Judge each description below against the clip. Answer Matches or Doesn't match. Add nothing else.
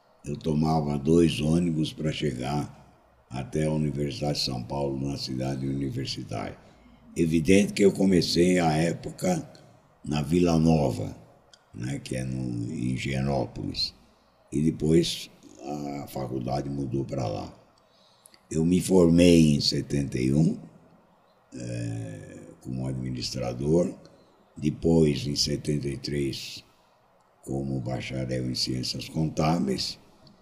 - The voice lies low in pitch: Matches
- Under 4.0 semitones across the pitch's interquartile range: Matches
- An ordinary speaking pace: Doesn't match